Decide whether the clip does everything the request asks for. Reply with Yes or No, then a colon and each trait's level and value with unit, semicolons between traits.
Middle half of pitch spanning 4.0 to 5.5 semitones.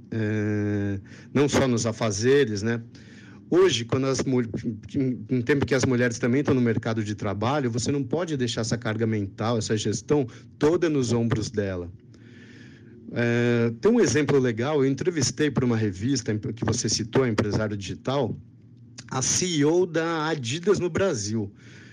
No: average, 3.3 semitones